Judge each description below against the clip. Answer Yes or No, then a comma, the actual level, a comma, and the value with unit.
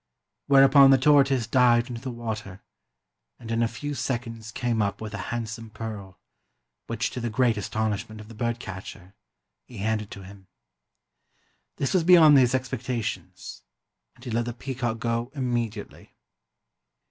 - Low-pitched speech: Yes, low, 115 Hz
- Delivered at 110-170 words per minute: Yes, average, 160 wpm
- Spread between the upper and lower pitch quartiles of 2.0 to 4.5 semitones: Yes, average, 2.8 semitones